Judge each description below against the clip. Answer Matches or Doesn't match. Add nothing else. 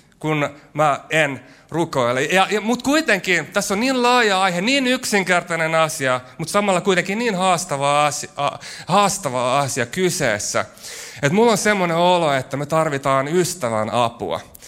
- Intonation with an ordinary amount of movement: Doesn't match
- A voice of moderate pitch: Matches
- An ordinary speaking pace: Matches